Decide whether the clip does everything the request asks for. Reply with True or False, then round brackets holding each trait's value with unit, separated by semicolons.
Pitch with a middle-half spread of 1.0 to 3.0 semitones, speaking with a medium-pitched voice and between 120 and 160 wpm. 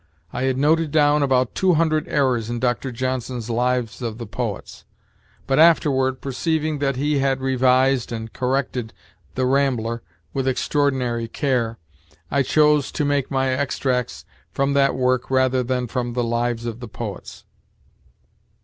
False (2.4 semitones; 130 Hz; 150 wpm)